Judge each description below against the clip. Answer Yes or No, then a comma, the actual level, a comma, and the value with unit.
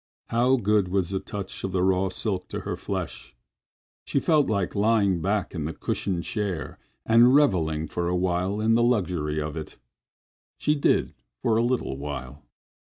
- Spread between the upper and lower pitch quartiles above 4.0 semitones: Yes, average, 4.6 semitones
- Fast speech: No, average, 175 wpm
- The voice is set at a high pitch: No, very low, 95 Hz